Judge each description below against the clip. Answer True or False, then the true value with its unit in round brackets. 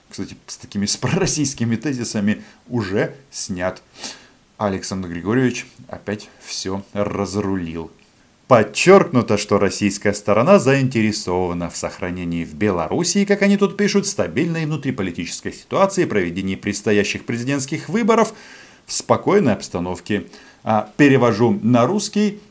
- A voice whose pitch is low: True (110 Hz)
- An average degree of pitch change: False (7.3 semitones)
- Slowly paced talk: True (100 wpm)